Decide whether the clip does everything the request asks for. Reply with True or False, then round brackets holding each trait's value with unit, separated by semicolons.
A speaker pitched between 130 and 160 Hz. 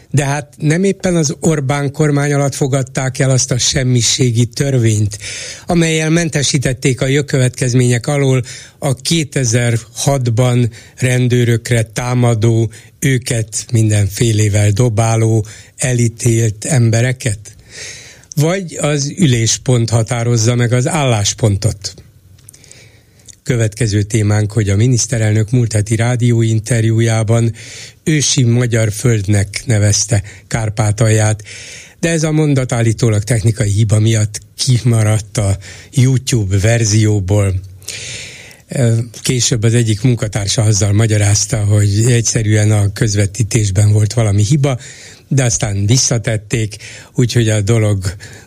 False (115 Hz)